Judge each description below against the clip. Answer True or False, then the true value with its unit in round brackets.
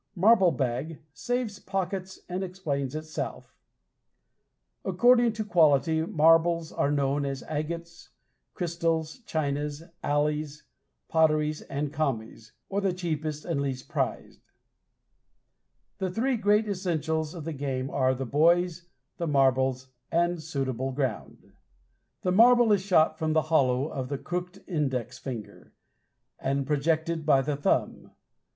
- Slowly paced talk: True (125 wpm)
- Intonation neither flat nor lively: True (4.0 semitones)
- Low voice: False (155 Hz)